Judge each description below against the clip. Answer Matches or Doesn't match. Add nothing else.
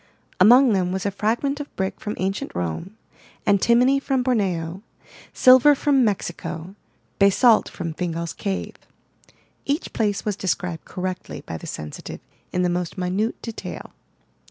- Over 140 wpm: Doesn't match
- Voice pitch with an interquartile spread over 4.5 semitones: Matches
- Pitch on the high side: Matches